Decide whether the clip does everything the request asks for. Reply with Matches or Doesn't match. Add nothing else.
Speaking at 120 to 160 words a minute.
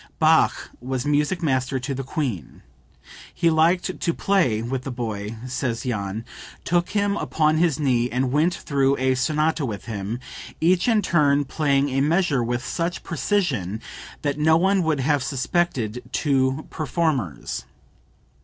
Matches